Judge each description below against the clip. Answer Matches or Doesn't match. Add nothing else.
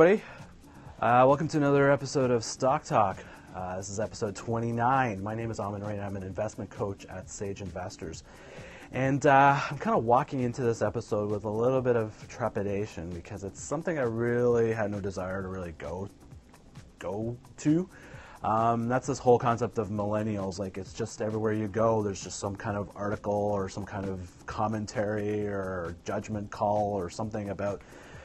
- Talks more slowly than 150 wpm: Doesn't match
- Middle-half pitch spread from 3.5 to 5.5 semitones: Doesn't match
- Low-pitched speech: Matches